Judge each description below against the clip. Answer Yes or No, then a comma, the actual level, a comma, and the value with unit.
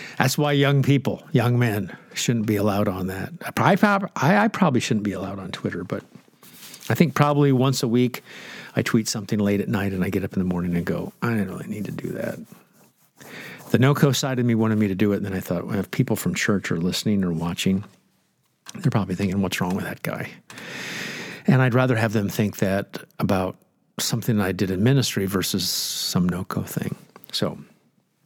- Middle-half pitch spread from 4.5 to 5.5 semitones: Yes, average, 5.1 semitones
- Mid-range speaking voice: No, low, 110 Hz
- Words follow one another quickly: Yes, fast, 210 wpm